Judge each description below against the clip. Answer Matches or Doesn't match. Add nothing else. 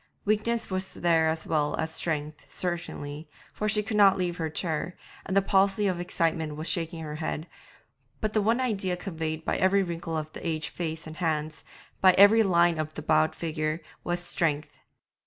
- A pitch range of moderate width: Matches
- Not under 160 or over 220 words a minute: Matches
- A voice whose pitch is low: Doesn't match